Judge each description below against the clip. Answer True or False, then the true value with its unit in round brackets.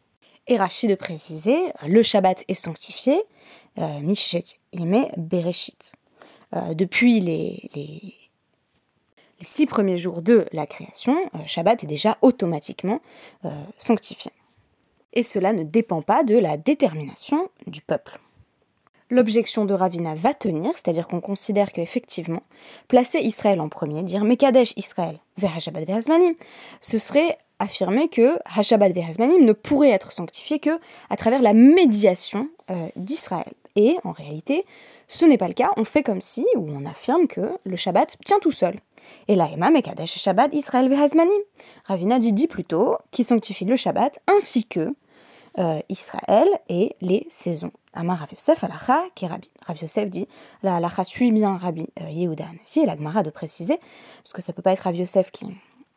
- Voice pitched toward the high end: True (205 Hz)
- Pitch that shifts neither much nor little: False (6.2 semitones)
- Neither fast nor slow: True (160 wpm)